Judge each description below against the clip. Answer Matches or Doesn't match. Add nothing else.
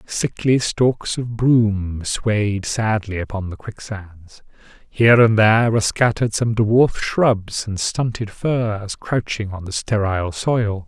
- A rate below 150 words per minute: Matches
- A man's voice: Matches